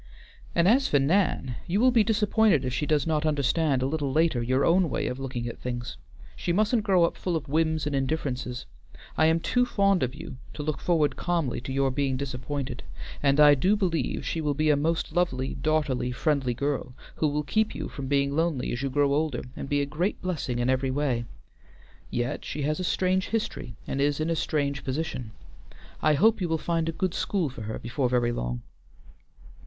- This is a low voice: No, medium, 145 Hz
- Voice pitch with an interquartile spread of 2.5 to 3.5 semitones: No, average, 4.2 semitones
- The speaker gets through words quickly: Yes, fast, 210 wpm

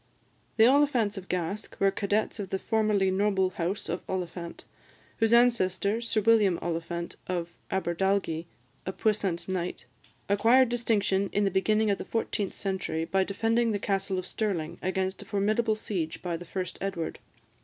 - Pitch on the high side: Yes, high, 195 Hz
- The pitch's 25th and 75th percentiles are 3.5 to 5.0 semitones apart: No, average, 2.8 semitones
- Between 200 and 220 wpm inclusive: No, average, 155 wpm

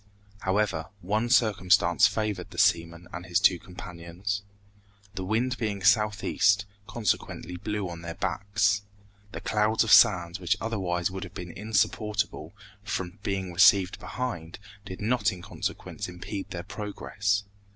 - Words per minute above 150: No, slow, 135 wpm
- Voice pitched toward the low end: Yes, low, 100 Hz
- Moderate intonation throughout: Yes, average, 3.0 semitones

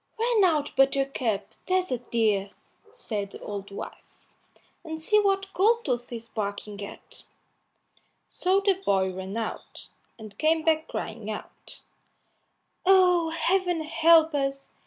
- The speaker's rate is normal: No, slow, 125 wpm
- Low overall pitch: No, very high, 295 Hz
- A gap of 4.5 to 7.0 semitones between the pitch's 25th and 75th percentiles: No, wide, 9.0 semitones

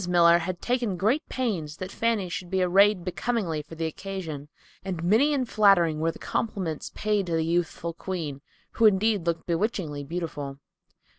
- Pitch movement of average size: Yes, average, 4.1 semitones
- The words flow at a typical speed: Yes, average, 165 wpm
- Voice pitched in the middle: Yes, medium, 180 Hz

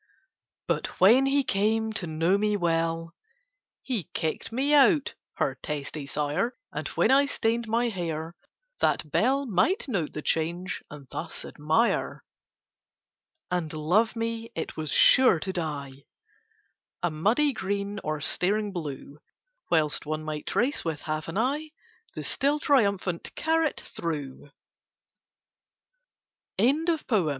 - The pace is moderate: No, slow, 120 wpm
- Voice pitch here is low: No, medium, 185 Hz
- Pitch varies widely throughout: Yes, wide, 6.9 semitones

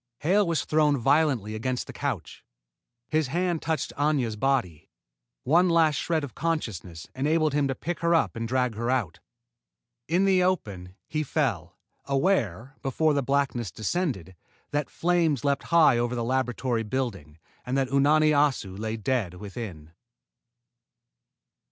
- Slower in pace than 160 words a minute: Yes, average, 140 wpm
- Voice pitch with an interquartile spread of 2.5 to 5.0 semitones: No, wide, 5.6 semitones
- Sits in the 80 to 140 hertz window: Yes, low, 135 Hz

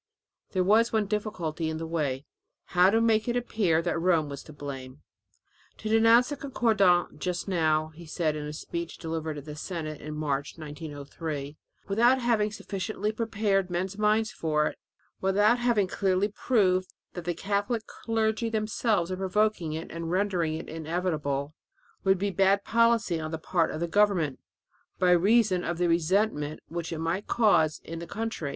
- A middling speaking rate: Yes, average, 170 wpm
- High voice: No, medium, 180 Hz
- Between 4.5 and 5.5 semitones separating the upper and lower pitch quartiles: Yes, average, 5.1 semitones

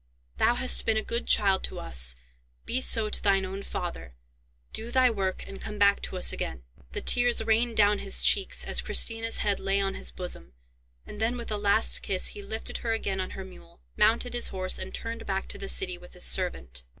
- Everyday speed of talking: No, fast, 215 wpm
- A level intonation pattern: No, average, 3.3 semitones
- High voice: Yes, high, 200 Hz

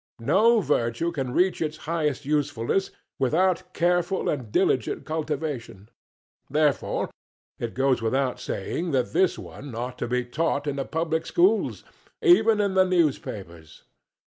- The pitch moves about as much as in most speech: No, wide, 5.9 semitones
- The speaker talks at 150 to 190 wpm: No, slow, 135 wpm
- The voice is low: No, medium, 150 Hz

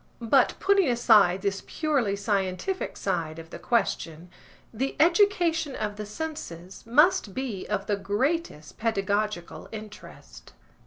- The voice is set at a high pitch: Yes, high, 210 Hz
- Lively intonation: Yes, wide, 7.0 semitones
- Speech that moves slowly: Yes, slow, 120 wpm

